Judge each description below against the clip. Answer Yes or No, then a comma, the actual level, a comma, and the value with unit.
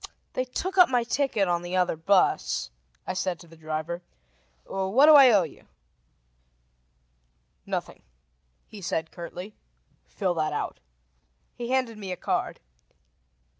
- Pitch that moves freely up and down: Yes, wide, 6.1 semitones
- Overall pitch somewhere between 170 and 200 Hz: Yes, high, 190 Hz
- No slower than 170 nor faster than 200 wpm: No, slow, 135 wpm